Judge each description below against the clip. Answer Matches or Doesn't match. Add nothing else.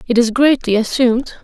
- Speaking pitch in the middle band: Doesn't match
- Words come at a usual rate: Matches